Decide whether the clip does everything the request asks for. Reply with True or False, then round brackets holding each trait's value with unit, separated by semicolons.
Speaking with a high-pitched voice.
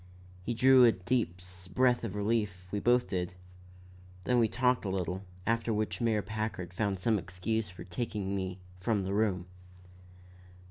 False (105 Hz)